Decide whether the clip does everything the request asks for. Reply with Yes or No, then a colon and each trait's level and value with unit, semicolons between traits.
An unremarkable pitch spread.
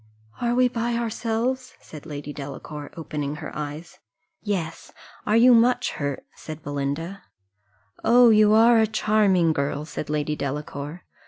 No: wide, 7.4 semitones